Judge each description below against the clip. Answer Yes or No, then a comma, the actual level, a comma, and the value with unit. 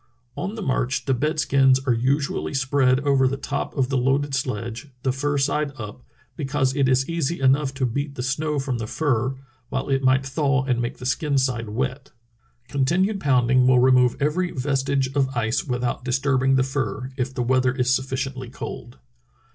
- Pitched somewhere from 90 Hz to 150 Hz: Yes, low, 135 Hz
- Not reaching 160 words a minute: No, average, 185 wpm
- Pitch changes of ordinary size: No, narrow, 1.7 semitones